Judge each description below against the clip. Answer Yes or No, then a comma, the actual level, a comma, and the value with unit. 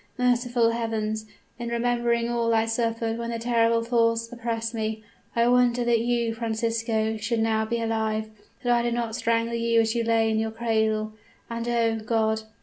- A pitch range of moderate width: No, narrow, 1.0 semitones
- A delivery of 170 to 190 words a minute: Yes, average, 175 wpm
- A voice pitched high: Yes, high, 230 Hz